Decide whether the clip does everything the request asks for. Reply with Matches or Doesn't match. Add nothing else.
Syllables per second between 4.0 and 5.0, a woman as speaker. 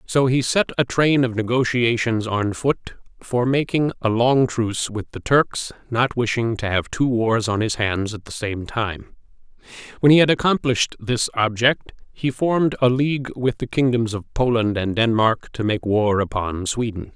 Doesn't match